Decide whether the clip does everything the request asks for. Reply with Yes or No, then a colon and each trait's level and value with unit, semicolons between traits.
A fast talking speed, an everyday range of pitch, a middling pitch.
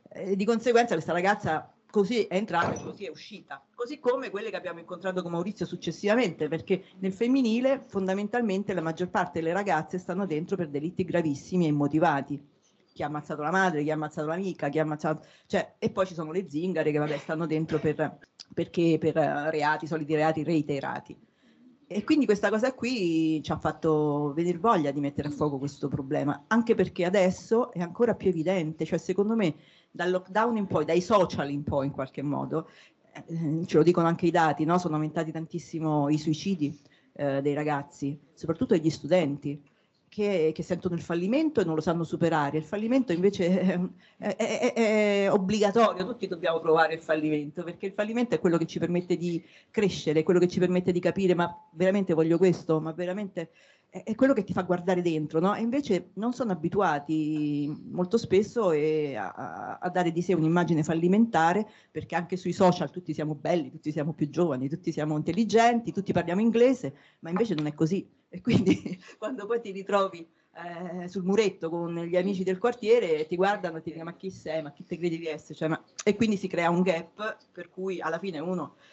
Yes: fast, 195 wpm; average, 3.9 semitones; medium, 175 Hz